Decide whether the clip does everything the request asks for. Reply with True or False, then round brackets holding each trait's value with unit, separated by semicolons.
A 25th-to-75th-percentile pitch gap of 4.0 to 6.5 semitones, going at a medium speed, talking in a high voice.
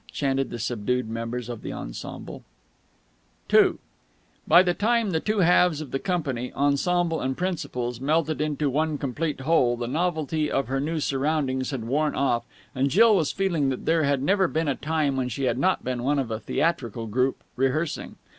False (4.3 semitones; 185 wpm; 140 Hz)